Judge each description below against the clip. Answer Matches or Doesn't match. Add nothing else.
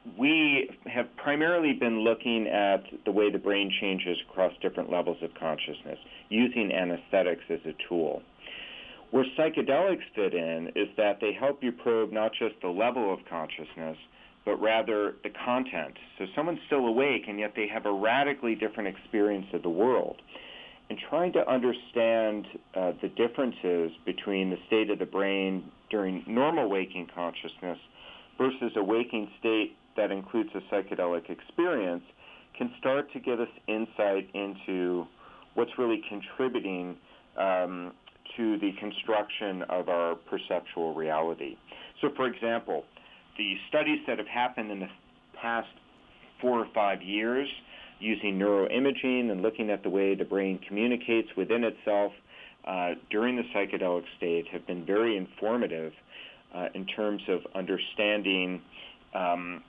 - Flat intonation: Doesn't match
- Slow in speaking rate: Doesn't match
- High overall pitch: Doesn't match